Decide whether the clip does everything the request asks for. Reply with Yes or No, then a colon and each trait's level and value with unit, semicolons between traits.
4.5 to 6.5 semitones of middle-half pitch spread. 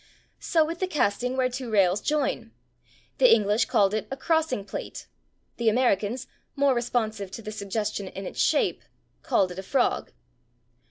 Yes: average, 5.0 semitones